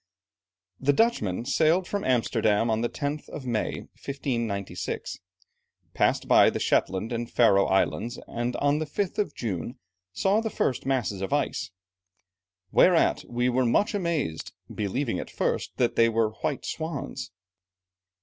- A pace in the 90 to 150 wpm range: Yes, average, 140 wpm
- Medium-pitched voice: No, low, 125 Hz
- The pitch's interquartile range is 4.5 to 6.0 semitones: Yes, average, 5.1 semitones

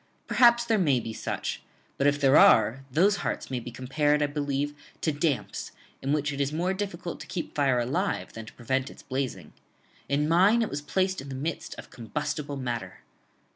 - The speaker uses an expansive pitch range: No, average, 4.0 semitones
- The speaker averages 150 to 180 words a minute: No, average, 195 wpm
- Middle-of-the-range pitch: Yes, medium, 145 Hz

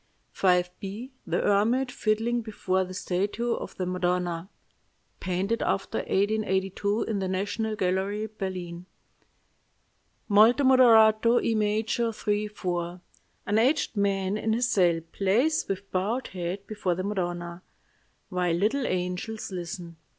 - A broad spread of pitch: No, average, 3.2 semitones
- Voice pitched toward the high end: Yes, high, 200 Hz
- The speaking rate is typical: No, slow, 120 wpm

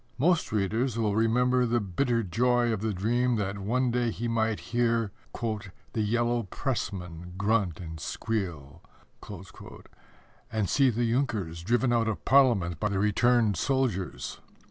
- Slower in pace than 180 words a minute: Yes, average, 140 wpm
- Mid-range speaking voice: No, low, 115 Hz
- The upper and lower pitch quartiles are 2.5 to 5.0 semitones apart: Yes, average, 3.7 semitones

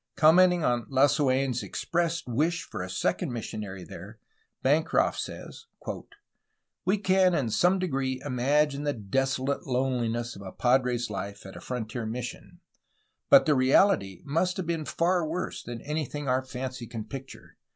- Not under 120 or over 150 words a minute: Yes, average, 145 wpm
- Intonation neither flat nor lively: Yes, average, 5.0 semitones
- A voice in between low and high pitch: No, low, 130 Hz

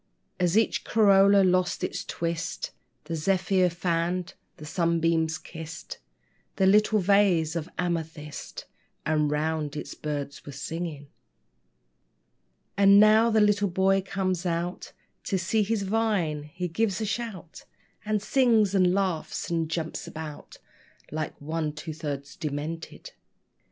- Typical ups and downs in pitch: Yes, average, 3.8 semitones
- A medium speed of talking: No, slow, 125 wpm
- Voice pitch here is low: No, medium, 175 Hz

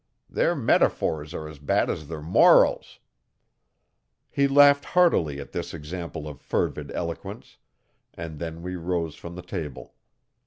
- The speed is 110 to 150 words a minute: Yes, average, 140 wpm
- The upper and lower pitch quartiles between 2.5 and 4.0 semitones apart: Yes, average, 2.9 semitones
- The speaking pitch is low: Yes, very low, 80 Hz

